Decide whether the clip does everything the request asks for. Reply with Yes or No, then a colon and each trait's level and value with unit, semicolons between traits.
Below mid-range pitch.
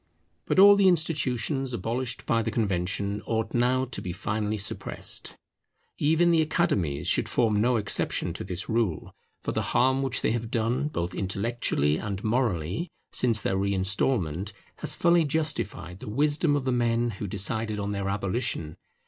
Yes: low, 115 Hz